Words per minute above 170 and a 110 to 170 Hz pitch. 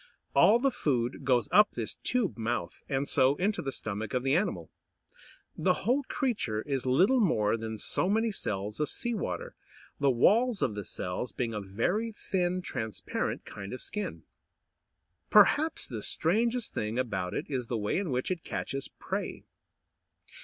No: average, 165 wpm; low, 135 Hz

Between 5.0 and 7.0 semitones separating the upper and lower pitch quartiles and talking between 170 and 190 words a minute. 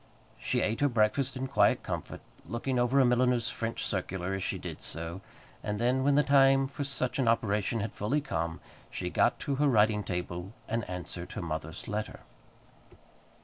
Yes: wide, 5.5 semitones; average, 180 wpm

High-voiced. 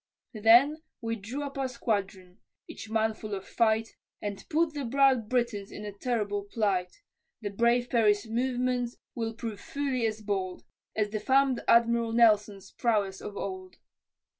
Yes: high, 225 Hz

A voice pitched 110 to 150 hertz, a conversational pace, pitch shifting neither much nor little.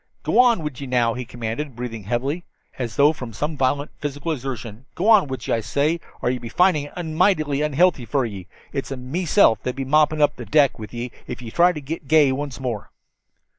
No: medium, 140 Hz; fast, 210 wpm; average, 4.0 semitones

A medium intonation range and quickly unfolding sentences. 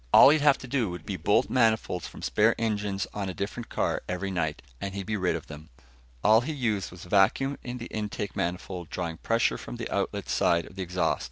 Yes: average, 4.1 semitones; fast, 225 wpm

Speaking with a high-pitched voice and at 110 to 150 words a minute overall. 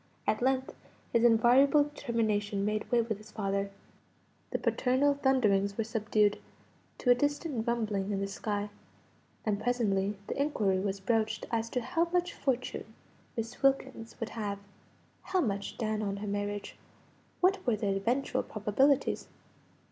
Yes: high, 225 Hz; average, 145 wpm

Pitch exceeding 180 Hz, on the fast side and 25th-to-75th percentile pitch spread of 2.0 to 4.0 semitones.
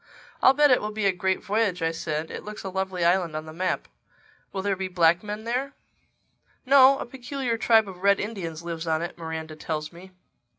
No: high, 190 Hz; fast, 210 wpm; average, 4.6 semitones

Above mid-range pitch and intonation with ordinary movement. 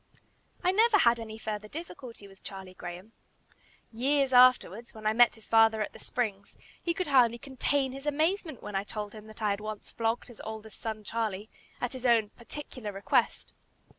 Yes: high, 225 Hz; average, 3.6 semitones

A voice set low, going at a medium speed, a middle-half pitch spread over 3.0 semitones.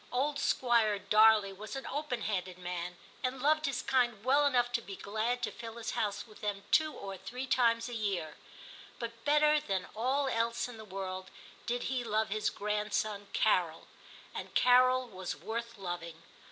No: high, 225 Hz; average, 175 wpm; average, 4.0 semitones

